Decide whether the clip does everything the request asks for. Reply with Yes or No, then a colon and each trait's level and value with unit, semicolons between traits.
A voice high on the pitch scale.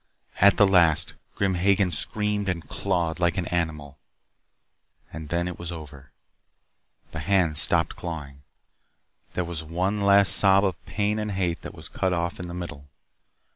No: very low, 85 Hz